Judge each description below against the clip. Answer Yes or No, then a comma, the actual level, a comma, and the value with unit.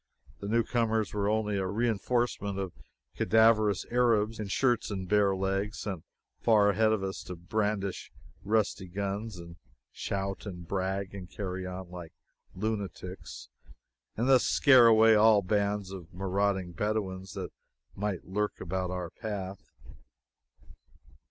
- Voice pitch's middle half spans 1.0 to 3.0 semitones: Yes, narrow, 2.5 semitones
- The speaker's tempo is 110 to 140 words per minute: Yes, slow, 135 wpm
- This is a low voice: Yes, low, 100 Hz